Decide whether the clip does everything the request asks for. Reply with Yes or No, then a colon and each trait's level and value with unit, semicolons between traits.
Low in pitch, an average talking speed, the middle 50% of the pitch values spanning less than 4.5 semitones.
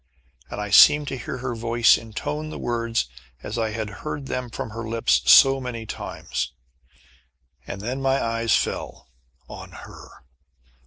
Yes: low, 115 Hz; average, 155 wpm; average, 2.9 semitones